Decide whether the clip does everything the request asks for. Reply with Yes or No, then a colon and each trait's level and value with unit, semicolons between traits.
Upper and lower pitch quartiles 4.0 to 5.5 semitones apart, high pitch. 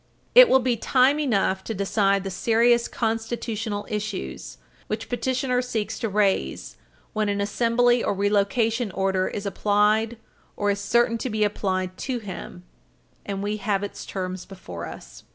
No: average, 3.1 semitones; high, 210 Hz